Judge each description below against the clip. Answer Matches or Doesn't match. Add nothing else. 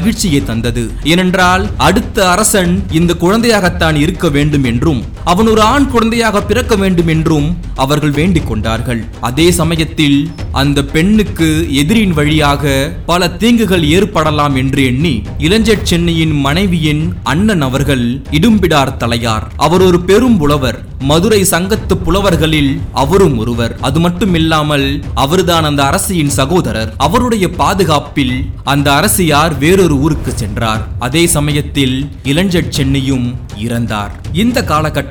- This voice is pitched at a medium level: Matches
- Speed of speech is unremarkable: Matches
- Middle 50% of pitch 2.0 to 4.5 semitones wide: Doesn't match